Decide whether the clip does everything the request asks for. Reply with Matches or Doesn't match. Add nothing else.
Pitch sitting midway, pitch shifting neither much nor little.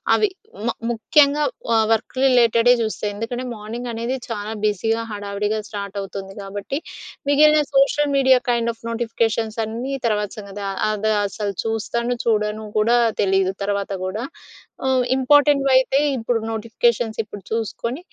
Doesn't match